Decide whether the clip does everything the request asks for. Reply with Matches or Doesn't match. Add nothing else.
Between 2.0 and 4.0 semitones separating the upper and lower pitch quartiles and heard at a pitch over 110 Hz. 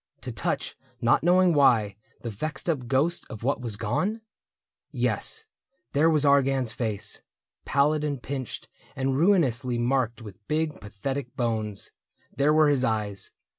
Doesn't match